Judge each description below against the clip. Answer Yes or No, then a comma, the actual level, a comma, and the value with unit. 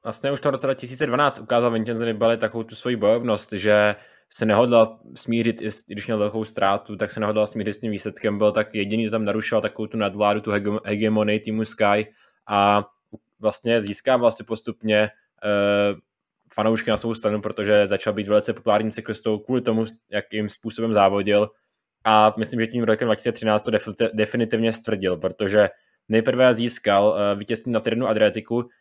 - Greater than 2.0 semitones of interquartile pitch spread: No, narrow, 1.6 semitones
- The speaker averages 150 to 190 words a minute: Yes, average, 165 wpm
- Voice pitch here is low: Yes, low, 110 Hz